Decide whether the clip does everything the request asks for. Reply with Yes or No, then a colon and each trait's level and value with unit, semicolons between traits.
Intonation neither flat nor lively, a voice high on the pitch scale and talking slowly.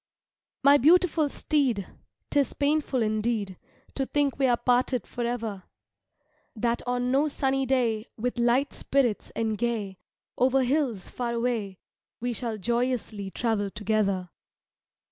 Yes: average, 3.6 semitones; high, 240 Hz; slow, 125 wpm